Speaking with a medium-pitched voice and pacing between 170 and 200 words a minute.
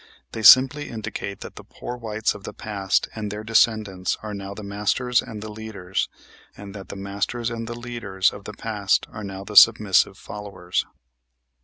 No: low, 105 Hz; average, 180 wpm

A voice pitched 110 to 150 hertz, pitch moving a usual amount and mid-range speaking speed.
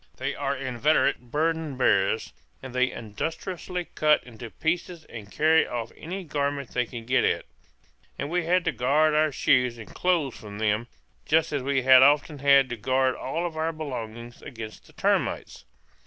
Yes: low, 135 Hz; average, 4.6 semitones; average, 170 wpm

